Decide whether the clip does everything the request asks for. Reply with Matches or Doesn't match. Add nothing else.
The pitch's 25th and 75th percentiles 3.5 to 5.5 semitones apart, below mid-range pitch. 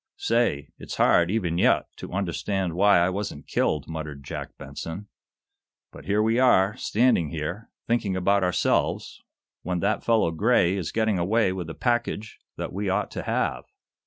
Matches